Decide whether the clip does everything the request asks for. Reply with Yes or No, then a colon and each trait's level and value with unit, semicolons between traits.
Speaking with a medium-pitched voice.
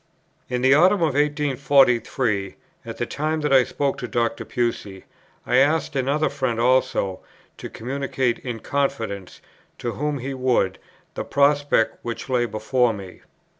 No: low, 130 Hz